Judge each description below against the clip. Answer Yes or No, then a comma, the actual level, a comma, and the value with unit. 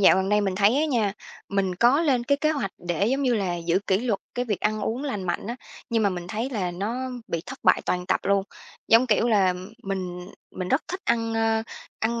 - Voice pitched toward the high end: Yes, high, 210 Hz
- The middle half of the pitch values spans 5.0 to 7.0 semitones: No, average, 4.1 semitones